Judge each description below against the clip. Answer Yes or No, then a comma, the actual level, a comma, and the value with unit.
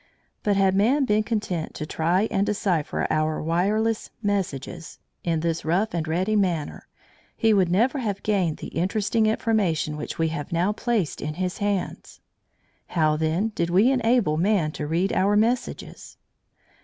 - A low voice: No, high, 190 Hz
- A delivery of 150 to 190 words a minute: Yes, average, 155 wpm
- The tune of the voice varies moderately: Yes, average, 4.7 semitones